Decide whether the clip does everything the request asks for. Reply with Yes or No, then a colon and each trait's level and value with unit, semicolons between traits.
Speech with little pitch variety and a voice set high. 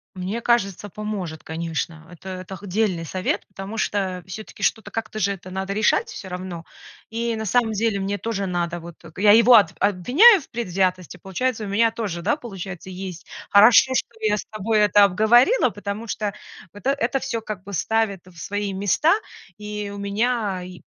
No: average, 3.3 semitones; high, 200 Hz